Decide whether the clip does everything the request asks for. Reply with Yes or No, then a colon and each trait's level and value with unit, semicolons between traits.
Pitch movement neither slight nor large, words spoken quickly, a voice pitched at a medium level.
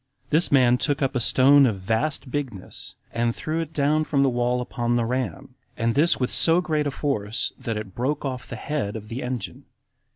No: average, 3.8 semitones; fast, 215 wpm; low, 130 Hz